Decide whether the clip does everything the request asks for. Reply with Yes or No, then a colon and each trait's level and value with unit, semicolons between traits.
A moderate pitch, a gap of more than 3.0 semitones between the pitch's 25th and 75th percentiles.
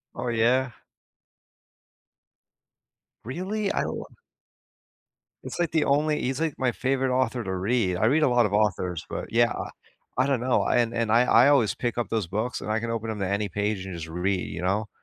No: low, 115 Hz; average, 4.2 semitones